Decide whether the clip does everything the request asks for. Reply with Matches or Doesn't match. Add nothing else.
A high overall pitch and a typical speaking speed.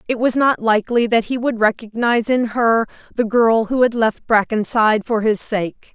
Matches